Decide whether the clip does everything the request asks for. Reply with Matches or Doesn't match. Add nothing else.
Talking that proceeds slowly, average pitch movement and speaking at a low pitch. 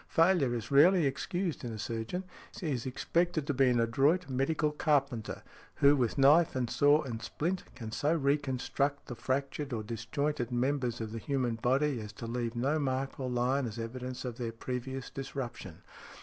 Doesn't match